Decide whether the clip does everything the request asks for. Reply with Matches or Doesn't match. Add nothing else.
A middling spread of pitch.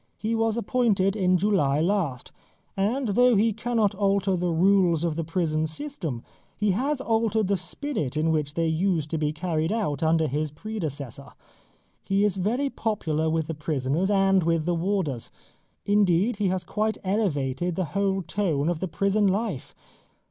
Matches